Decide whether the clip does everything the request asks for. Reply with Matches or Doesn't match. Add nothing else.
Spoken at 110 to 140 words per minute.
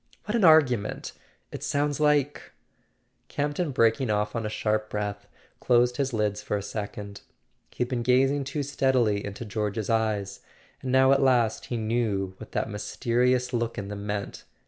Doesn't match